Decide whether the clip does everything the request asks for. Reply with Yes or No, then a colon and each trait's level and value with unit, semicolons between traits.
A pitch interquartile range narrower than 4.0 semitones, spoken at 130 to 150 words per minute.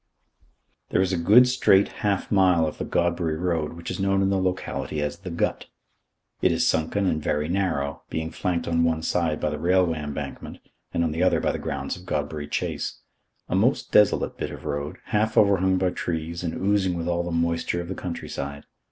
No: average, 3.0 semitones; fast, 205 wpm